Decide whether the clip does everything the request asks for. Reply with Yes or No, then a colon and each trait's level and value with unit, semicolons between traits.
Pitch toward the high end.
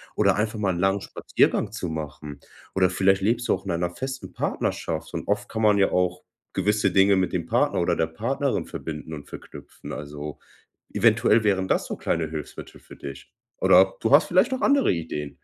No: very low, 95 Hz